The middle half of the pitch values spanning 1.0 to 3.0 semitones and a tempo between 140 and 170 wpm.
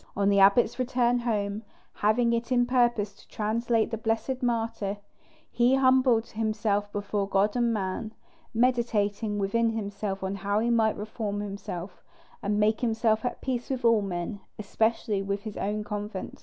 Yes: narrow, 2.5 semitones; average, 155 wpm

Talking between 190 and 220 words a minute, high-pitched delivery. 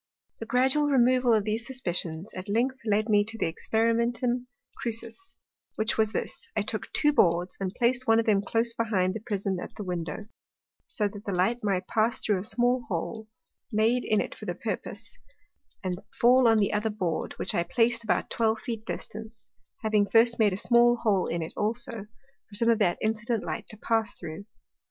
Yes: average, 195 wpm; high, 220 Hz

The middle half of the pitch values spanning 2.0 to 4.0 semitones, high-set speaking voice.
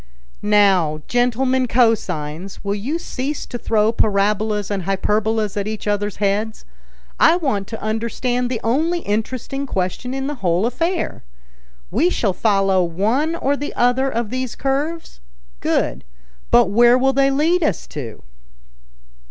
No: average, 4.8 semitones; high, 225 Hz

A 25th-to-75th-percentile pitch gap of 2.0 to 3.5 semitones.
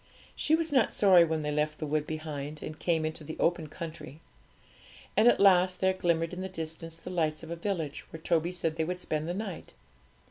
Yes: average, 2.7 semitones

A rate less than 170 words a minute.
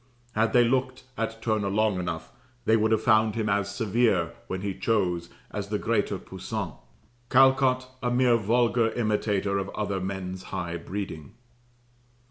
Yes: average, 150 wpm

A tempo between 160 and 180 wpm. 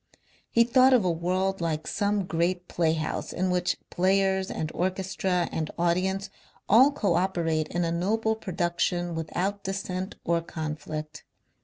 No: average, 140 wpm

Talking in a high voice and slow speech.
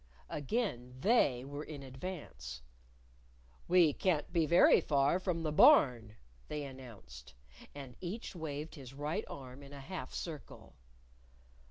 No: medium, 145 Hz; slow, 130 wpm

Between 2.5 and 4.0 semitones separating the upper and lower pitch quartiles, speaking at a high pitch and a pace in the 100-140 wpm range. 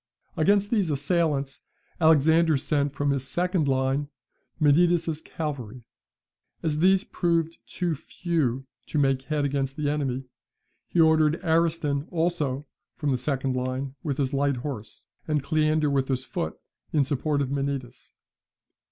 No: average, 3.0 semitones; medium, 145 Hz; slow, 135 wpm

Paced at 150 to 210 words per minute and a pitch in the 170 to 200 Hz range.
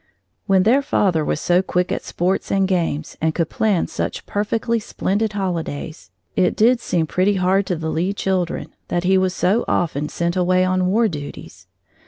Yes: average, 180 wpm; medium, 185 Hz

